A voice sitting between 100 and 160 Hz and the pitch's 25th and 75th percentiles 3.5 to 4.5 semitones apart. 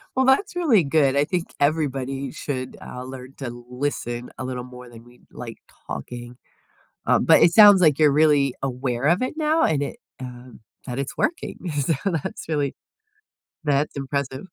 Yes: medium, 140 Hz; average, 3.8 semitones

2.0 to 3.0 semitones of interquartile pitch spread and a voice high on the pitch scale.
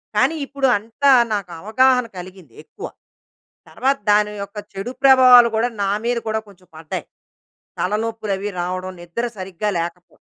No: average, 4.7 semitones; high, 210 Hz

